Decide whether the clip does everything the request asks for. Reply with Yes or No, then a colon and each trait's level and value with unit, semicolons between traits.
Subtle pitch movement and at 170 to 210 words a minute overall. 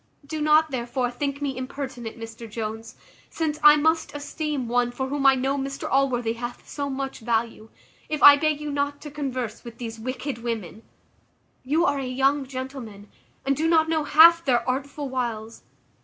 No: average, 3.3 semitones; average, 175 wpm